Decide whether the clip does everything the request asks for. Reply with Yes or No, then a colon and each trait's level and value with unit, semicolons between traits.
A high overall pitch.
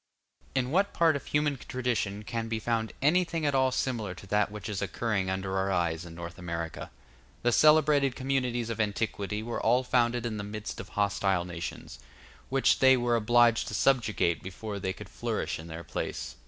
No: low, 110 Hz